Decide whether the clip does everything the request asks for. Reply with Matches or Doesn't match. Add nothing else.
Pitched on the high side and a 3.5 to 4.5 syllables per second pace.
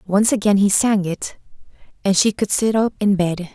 Doesn't match